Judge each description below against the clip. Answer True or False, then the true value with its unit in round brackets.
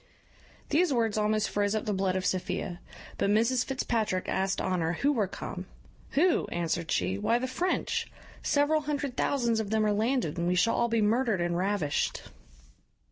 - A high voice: True (215 Hz)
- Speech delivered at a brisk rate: False (175 wpm)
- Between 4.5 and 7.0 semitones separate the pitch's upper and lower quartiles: True (5.3 semitones)